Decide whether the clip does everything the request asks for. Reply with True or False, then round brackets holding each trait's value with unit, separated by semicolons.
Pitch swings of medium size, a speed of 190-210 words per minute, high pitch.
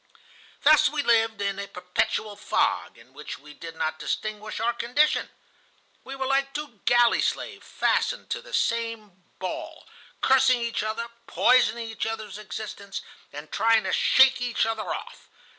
False (3.6 semitones; 155 wpm; 225 Hz)